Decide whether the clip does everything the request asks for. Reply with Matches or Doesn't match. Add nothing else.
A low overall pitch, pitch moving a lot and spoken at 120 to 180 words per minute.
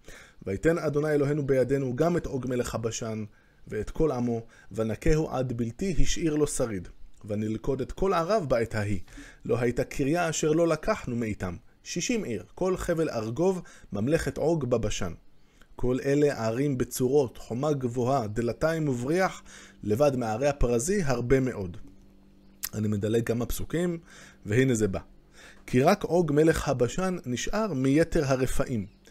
Matches